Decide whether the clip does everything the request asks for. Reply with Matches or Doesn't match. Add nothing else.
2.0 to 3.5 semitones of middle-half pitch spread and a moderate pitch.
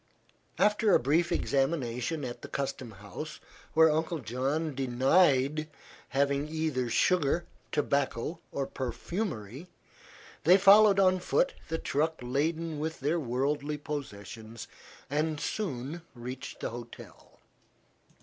Doesn't match